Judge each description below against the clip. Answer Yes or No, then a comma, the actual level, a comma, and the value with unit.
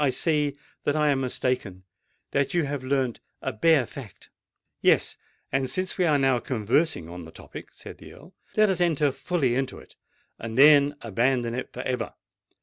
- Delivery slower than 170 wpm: No, average, 175 wpm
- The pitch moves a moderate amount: Yes, average, 3.7 semitones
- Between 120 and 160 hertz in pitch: Yes, low, 135 Hz